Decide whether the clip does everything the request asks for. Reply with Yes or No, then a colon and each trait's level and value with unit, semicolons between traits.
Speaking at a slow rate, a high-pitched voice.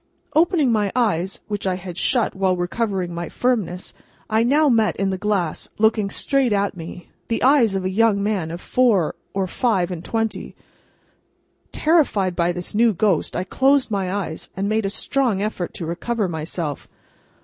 No: average, 170 wpm; high, 200 Hz